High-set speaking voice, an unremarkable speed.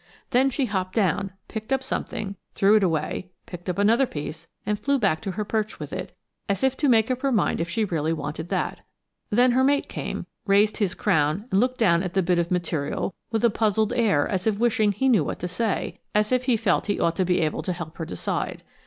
No: high, 200 Hz; fast, 235 wpm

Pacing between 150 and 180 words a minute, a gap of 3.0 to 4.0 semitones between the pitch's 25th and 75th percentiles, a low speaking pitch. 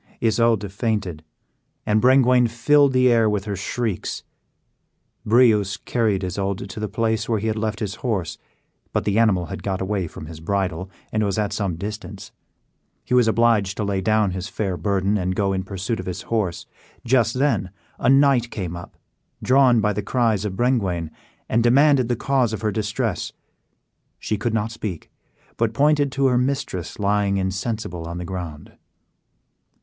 Yes: average, 170 wpm; average, 3.6 semitones; low, 105 Hz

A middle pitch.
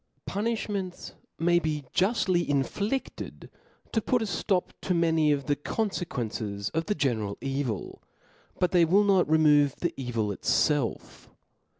Yes: medium, 160 Hz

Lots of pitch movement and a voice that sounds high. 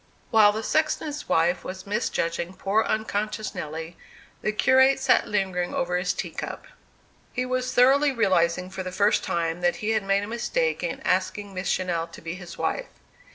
No: average, 4.4 semitones; high, 200 Hz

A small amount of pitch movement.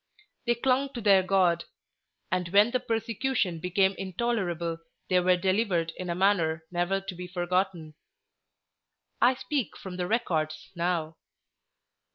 No: average, 3.8 semitones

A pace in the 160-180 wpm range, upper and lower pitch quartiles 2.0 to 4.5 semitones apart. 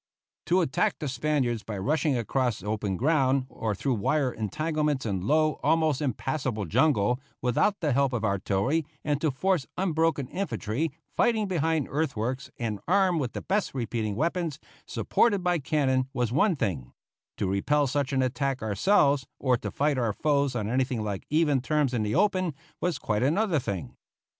No: average, 165 wpm; average, 5.2 semitones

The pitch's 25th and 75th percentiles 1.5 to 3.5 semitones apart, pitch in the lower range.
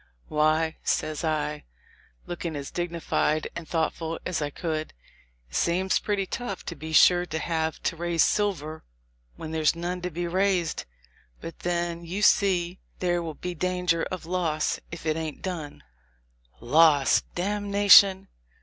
No: narrow, 2.4 semitones; medium, 170 Hz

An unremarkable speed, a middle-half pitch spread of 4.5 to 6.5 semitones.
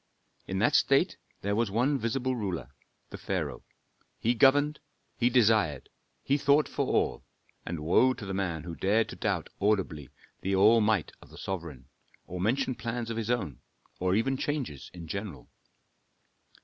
Yes: average, 160 wpm; average, 5.3 semitones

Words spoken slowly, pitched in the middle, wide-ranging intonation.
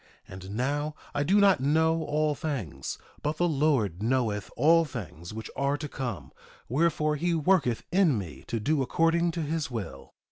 No: average, 170 wpm; medium, 145 Hz; wide, 5.7 semitones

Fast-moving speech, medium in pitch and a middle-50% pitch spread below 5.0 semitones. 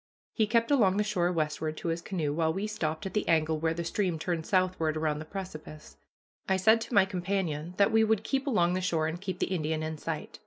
Yes: fast, 235 wpm; medium, 175 Hz; average, 4.0 semitones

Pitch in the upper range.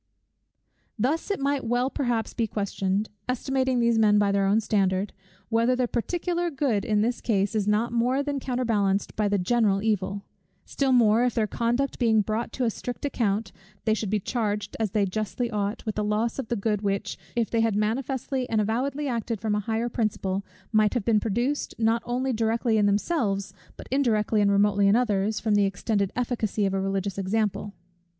Yes: high, 220 Hz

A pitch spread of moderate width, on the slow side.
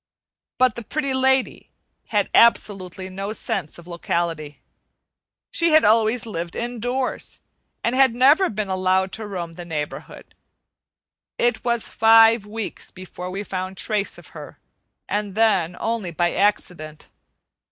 Yes: average, 4.5 semitones; slow, 130 wpm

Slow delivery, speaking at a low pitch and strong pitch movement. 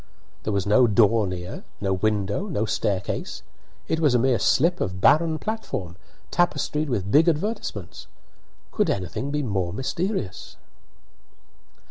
Yes: slow, 130 wpm; low, 115 Hz; wide, 8.0 semitones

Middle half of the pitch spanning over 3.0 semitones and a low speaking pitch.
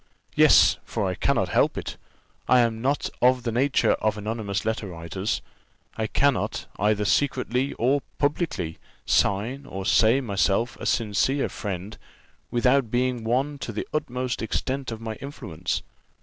Yes: average, 3.8 semitones; low, 115 Hz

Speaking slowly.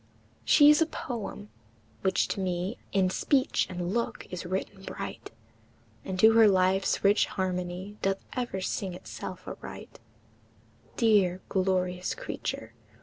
Yes: slow, 130 wpm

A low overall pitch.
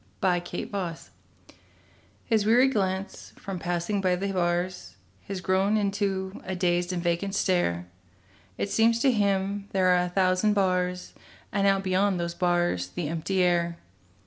No: medium, 185 Hz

